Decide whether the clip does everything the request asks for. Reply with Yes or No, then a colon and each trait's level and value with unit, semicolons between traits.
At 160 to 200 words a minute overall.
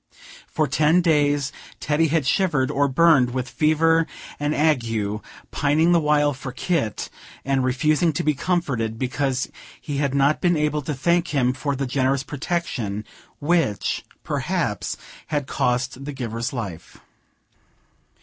No: average, 140 wpm